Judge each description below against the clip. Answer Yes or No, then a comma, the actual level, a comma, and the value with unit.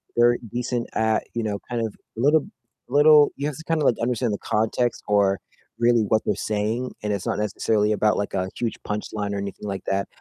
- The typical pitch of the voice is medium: No, low, 110 Hz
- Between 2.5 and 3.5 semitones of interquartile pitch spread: Yes, average, 2.9 semitones